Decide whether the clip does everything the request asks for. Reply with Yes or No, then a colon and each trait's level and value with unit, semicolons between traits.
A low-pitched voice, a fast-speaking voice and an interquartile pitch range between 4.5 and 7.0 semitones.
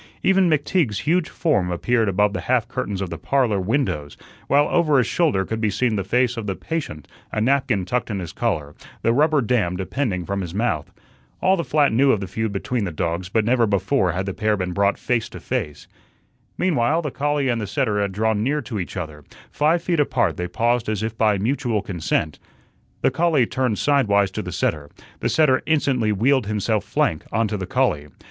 Yes: low, 110 Hz; fast, 210 wpm; wide, 5.6 semitones